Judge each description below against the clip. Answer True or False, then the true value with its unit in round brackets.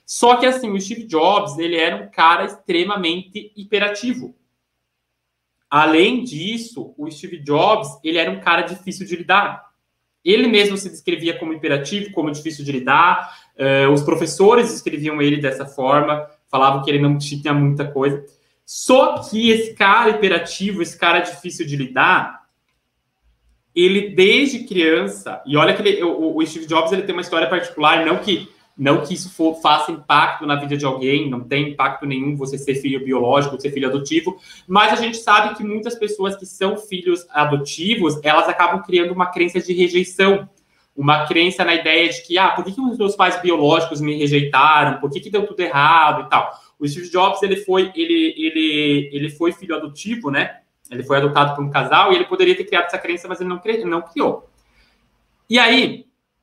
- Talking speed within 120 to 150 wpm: False (180 wpm)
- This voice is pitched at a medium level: True (170 Hz)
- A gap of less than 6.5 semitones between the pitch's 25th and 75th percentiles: True (5.5 semitones)